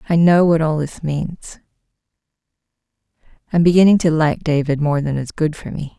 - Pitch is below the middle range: No, medium, 160 Hz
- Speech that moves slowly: No, average, 170 wpm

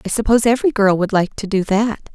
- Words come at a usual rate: No, fast, 250 wpm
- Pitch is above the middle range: Yes, high, 210 Hz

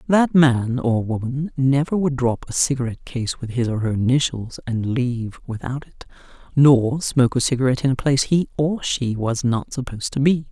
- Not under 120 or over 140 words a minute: No, average, 195 wpm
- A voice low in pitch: Yes, low, 130 Hz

